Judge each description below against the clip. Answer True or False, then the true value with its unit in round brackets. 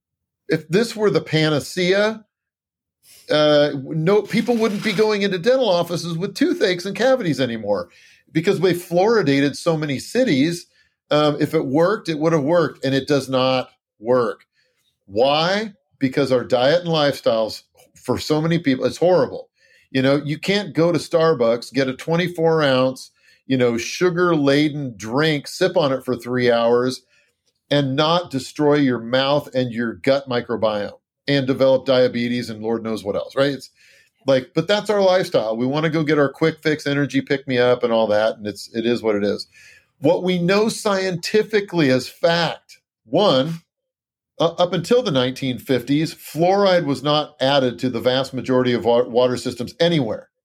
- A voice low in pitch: False (145 Hz)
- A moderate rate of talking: True (170 wpm)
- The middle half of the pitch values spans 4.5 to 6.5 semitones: True (5.5 semitones)